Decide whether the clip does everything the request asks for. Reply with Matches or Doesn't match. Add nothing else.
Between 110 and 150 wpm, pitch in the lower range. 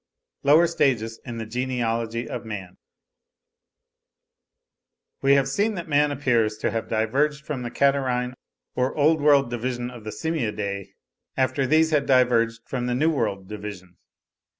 Matches